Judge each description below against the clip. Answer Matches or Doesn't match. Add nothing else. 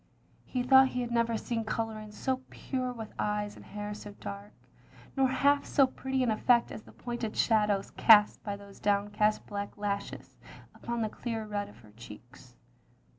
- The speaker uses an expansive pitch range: Doesn't match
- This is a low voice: Doesn't match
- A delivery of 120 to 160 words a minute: Doesn't match